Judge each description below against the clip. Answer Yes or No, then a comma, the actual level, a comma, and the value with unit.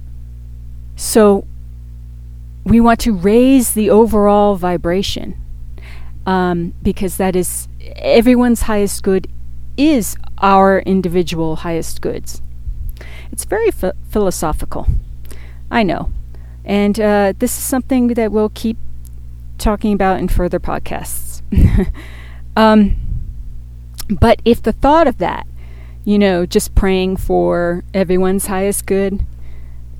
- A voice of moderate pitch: Yes, medium, 170 Hz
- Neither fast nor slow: No, slow, 110 wpm